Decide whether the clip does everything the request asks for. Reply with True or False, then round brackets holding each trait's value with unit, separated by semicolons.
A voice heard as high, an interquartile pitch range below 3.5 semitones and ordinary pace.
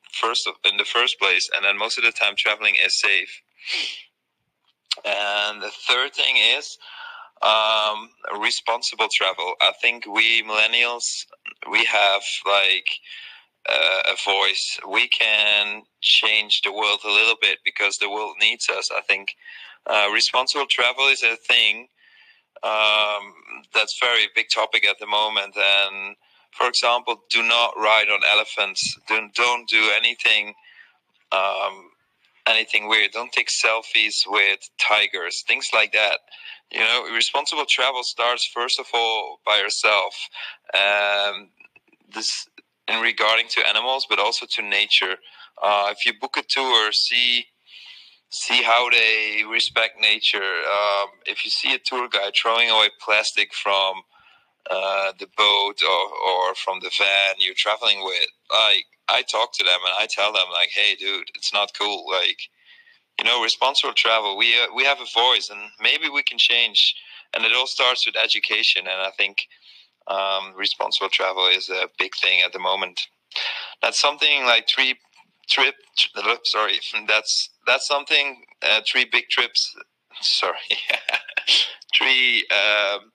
False (110 Hz; 3.0 semitones; 150 wpm)